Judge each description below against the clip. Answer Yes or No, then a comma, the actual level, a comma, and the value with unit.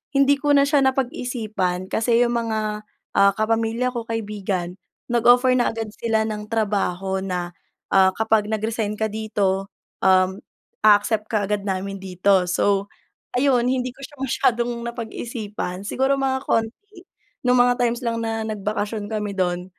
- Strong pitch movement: No, average, 3.3 semitones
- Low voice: No, high, 220 Hz